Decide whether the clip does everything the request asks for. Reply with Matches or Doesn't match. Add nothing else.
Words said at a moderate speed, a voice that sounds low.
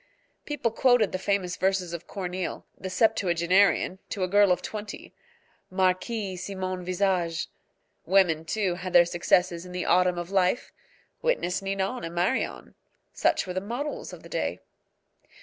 Doesn't match